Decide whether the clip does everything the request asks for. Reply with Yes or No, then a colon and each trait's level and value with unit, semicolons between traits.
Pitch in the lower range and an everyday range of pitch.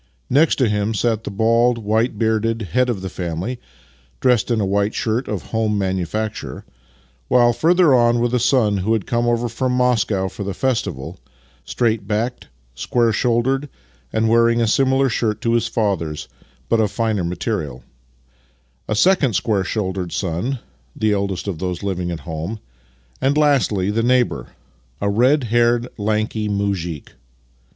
Yes: low, 110 Hz; average, 3.5 semitones